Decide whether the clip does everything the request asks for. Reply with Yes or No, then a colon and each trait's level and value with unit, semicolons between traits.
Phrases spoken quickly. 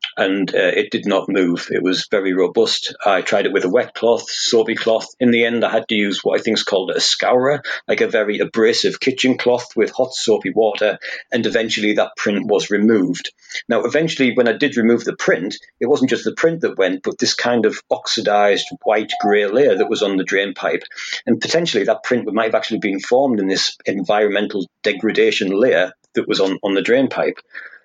Yes: fast, 215 wpm